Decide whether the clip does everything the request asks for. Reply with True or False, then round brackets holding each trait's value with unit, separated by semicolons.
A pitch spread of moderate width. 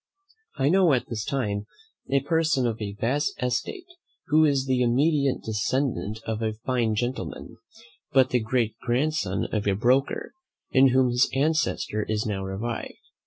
True (3.9 semitones)